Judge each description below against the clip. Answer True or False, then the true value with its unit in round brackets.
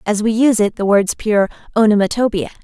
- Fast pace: False (185 wpm)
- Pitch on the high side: True (215 Hz)